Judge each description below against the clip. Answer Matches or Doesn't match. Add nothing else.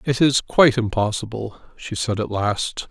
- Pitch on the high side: Doesn't match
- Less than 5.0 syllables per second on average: Matches